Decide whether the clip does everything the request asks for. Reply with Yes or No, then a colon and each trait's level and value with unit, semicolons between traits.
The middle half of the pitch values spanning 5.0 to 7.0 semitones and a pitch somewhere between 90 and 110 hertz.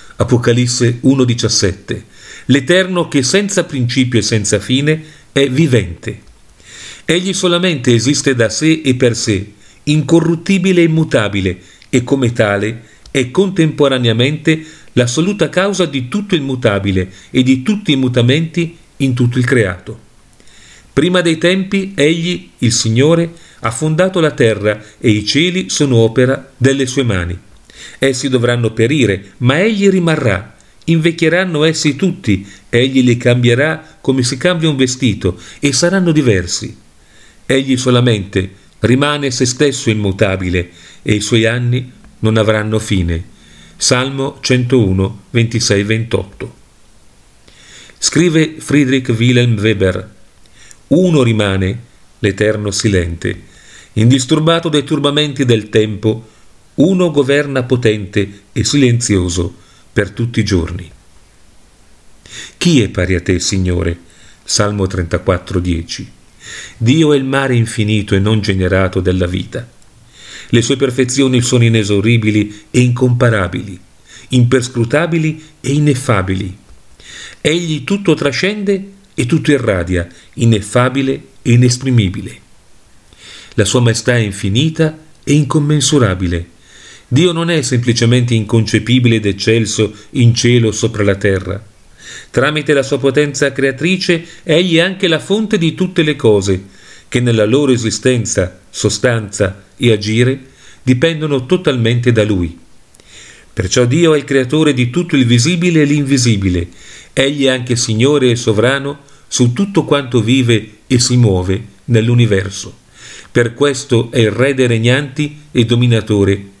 No: wide, 5.6 semitones; low, 120 Hz